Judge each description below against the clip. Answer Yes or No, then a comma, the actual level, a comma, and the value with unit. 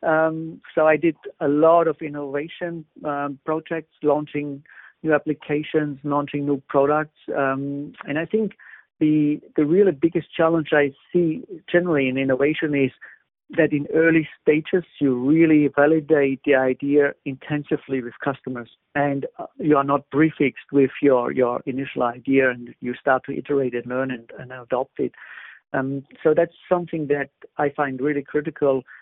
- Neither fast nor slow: Yes, average, 150 wpm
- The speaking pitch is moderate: Yes, medium, 145 Hz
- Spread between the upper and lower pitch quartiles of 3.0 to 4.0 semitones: No, narrow, 2.5 semitones